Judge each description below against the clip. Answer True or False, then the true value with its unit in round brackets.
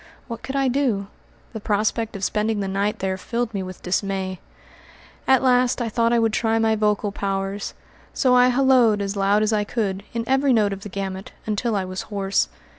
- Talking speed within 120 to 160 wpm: False (200 wpm)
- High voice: True (210 Hz)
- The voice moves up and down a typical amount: True (3.1 semitones)